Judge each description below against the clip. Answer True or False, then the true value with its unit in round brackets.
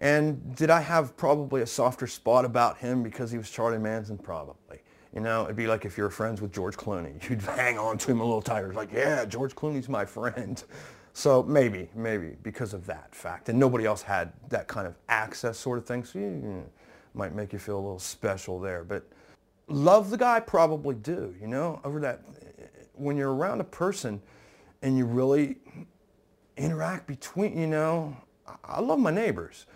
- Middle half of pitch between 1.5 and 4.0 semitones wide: False (5.1 semitones)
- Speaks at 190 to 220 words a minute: True (200 wpm)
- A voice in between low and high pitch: False (125 Hz)